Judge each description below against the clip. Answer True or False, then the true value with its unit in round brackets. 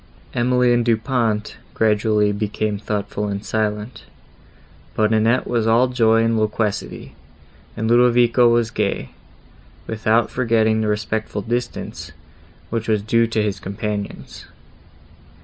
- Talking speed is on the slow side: True (120 wpm)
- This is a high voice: False (110 Hz)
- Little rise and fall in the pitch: True (1.8 semitones)